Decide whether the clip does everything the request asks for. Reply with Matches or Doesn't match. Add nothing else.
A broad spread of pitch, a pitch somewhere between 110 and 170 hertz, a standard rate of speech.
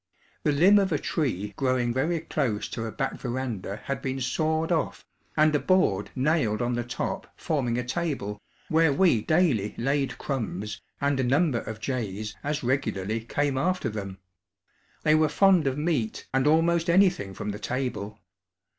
Matches